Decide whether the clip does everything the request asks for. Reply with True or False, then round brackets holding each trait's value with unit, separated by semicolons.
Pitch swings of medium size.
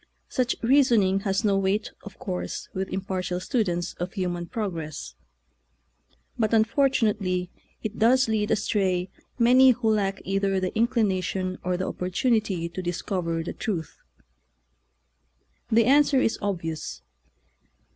True (3.5 semitones)